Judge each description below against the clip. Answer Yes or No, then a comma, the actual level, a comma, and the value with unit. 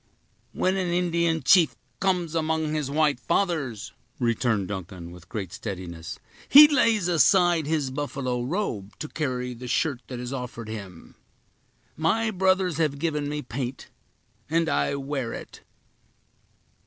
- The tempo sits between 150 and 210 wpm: No, slow, 135 wpm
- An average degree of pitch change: No, wide, 5.9 semitones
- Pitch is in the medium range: Yes, medium, 145 Hz